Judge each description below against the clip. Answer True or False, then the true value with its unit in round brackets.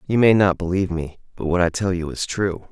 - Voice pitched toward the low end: True (90 Hz)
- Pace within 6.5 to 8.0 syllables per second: False (6.0 syllables/s)